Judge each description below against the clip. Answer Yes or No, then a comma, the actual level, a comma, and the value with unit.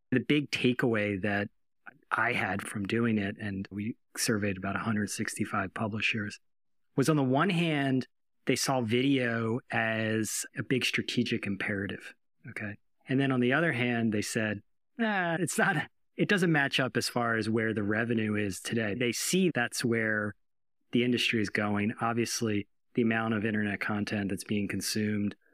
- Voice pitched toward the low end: Yes, low, 115 Hz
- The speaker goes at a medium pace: Yes, average, 160 wpm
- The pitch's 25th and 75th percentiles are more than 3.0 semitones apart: Yes, average, 3.6 semitones